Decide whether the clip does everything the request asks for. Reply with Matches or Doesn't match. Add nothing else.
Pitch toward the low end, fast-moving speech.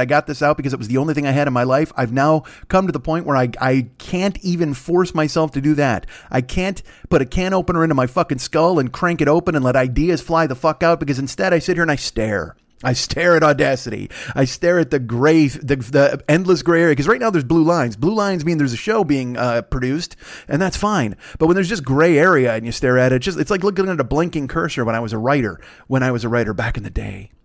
Doesn't match